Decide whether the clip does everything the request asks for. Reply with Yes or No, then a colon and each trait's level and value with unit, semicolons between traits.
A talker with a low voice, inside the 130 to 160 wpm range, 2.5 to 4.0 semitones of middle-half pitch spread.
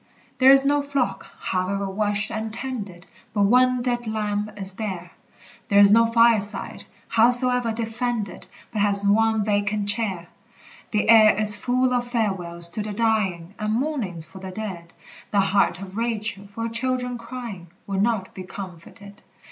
No: high, 215 Hz; average, 155 wpm; average, 3.0 semitones